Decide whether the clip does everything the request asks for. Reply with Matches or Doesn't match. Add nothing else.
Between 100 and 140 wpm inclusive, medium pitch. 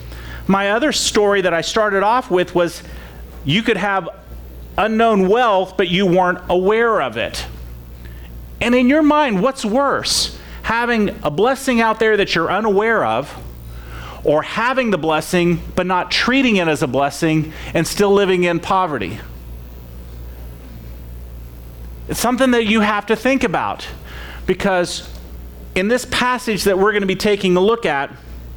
Doesn't match